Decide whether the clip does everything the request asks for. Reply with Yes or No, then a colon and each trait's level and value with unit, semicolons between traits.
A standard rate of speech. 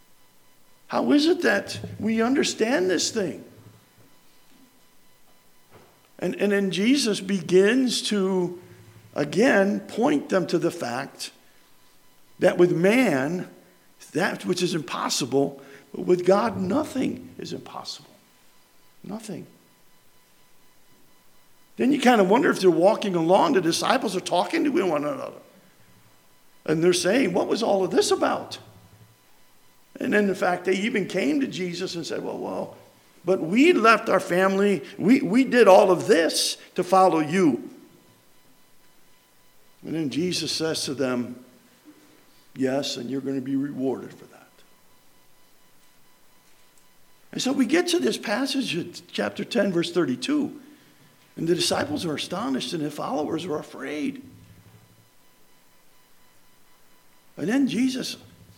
No: slow, 130 wpm